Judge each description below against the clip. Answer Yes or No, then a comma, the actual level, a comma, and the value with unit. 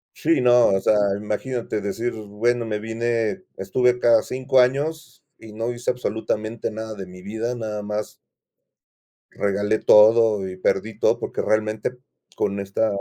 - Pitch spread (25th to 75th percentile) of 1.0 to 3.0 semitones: Yes, narrow, 2.6 semitones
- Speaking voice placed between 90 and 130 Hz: Yes, low, 110 Hz